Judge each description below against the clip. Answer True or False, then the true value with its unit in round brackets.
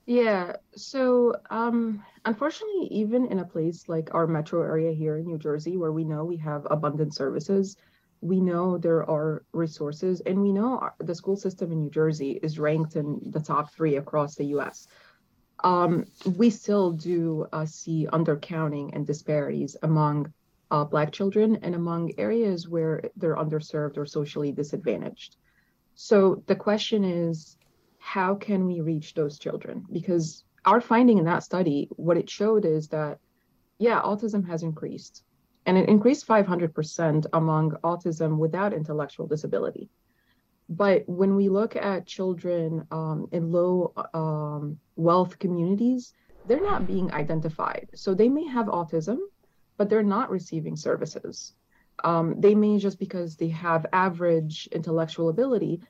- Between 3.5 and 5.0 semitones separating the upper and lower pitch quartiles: True (4.0 semitones)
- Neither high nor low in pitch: True (170 Hz)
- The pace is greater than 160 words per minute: False (150 wpm)